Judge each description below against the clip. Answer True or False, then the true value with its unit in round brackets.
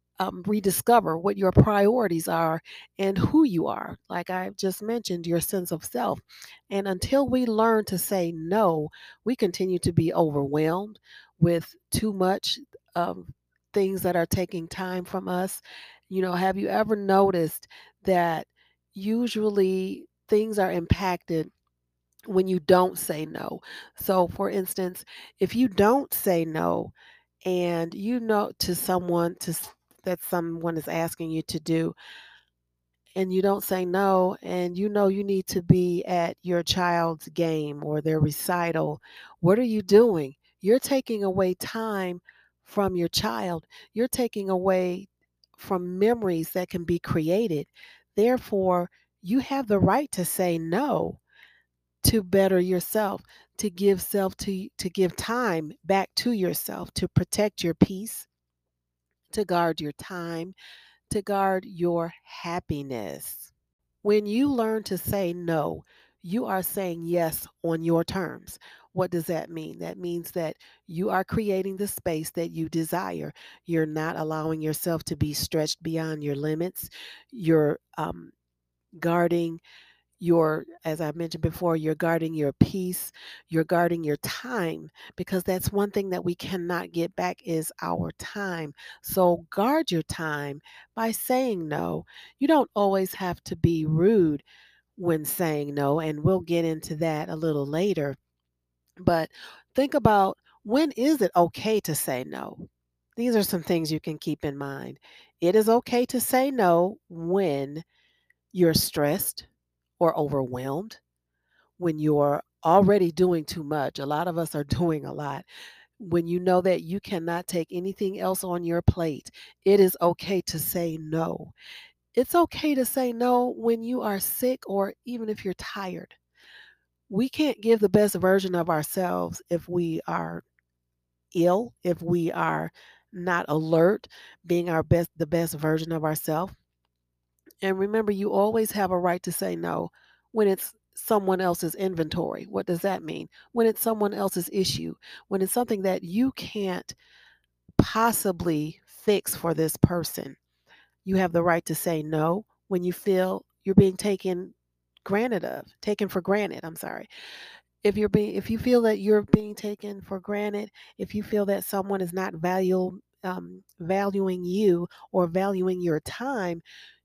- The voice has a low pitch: False (180 Hz)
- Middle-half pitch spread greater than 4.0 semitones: False (3.6 semitones)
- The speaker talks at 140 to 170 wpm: True (155 wpm)